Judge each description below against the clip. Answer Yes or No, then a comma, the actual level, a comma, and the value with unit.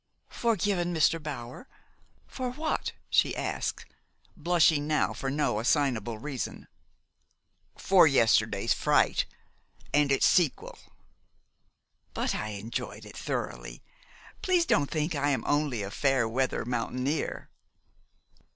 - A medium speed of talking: No, slow, 110 wpm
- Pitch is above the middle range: No, medium, 145 Hz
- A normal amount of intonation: Yes, average, 5.0 semitones